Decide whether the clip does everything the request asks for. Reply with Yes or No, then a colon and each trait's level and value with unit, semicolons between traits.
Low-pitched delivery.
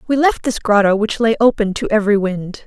No: high, 215 Hz